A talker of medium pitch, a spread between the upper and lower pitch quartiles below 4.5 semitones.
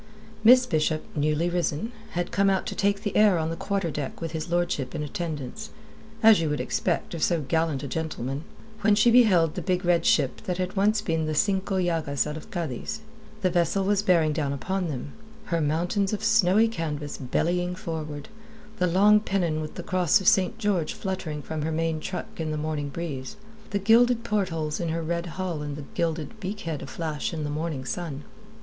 Yes: medium, 170 Hz; average, 3.9 semitones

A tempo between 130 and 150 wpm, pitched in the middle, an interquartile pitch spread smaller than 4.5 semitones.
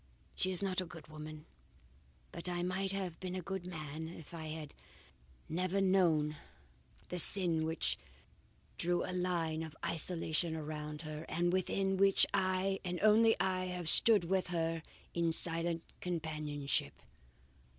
Yes: average, 145 wpm; medium, 175 Hz; average, 2.7 semitones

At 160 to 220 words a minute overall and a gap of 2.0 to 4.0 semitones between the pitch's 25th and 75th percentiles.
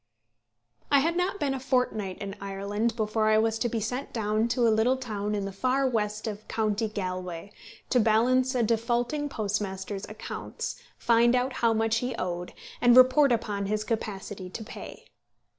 Yes: average, 165 wpm; average, 3.3 semitones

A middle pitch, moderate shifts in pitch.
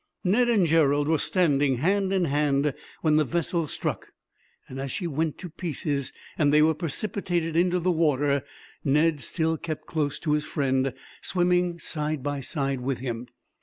Yes: medium, 155 Hz; average, 3.5 semitones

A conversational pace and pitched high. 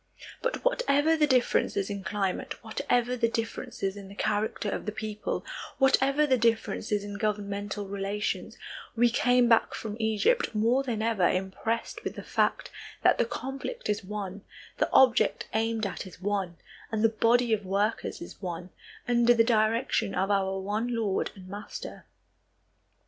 Yes: average, 155 wpm; high, 215 Hz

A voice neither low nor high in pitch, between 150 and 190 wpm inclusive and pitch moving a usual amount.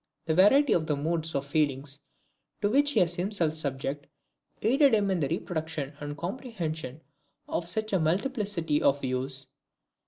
No: medium, 160 Hz; average, 155 wpm; wide, 5.8 semitones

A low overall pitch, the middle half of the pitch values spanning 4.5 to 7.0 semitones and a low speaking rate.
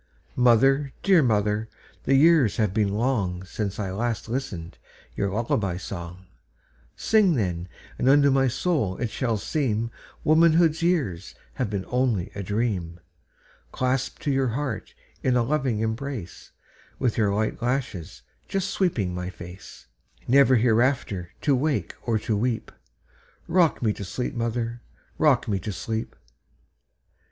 Yes: low, 115 Hz; average, 5.3 semitones; slow, 120 wpm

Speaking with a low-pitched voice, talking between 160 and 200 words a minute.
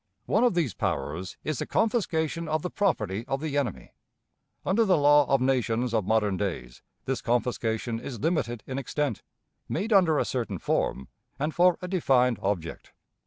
Yes: low, 130 Hz; average, 165 wpm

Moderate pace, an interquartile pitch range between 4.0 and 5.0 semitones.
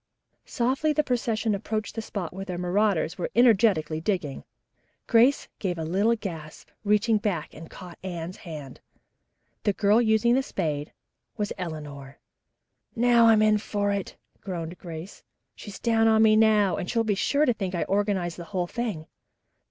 Yes: average, 160 wpm; average, 4.3 semitones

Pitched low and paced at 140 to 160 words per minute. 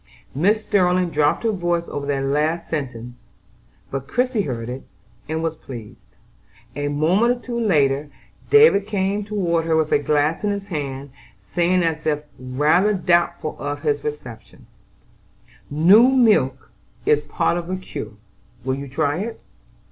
No: medium, 160 Hz; average, 150 wpm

